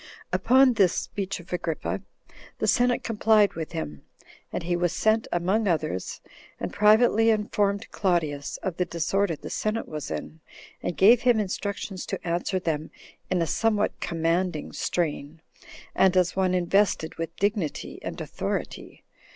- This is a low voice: No, medium, 185 Hz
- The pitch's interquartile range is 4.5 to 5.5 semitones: No, average, 4.0 semitones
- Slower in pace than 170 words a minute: Yes, average, 150 wpm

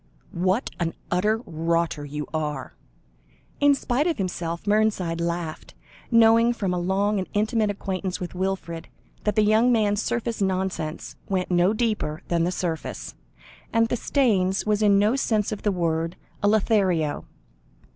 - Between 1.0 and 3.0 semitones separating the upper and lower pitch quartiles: No, average, 4.2 semitones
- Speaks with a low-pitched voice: No, high, 195 Hz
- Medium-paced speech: Yes, average, 150 wpm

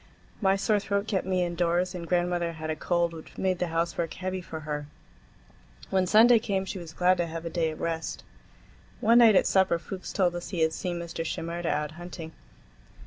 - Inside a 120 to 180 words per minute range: No, average, 200 wpm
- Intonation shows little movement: Yes, narrow, 2.2 semitones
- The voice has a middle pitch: Yes, medium, 175 Hz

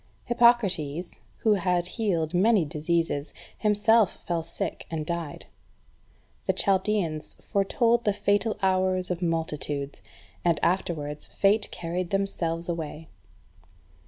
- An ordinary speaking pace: No, slow, 110 wpm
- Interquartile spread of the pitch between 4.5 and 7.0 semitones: No, average, 3.8 semitones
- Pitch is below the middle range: No, medium, 180 Hz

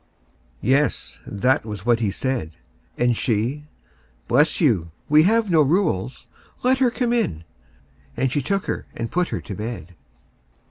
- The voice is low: Yes, low, 130 Hz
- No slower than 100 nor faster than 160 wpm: Yes, average, 150 wpm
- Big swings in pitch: Yes, wide, 7.6 semitones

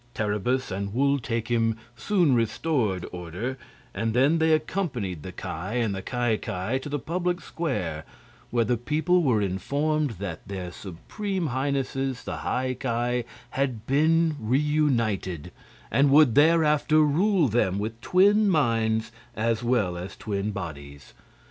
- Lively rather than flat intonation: Yes, wide, 6.3 semitones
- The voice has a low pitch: Yes, low, 120 Hz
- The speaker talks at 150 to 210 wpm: No, slow, 135 wpm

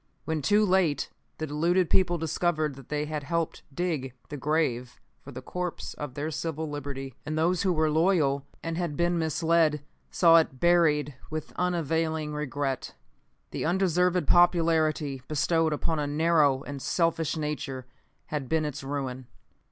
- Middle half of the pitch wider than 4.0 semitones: No, narrow, 2.6 semitones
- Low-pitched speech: No, medium, 155 Hz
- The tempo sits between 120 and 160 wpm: Yes, average, 150 wpm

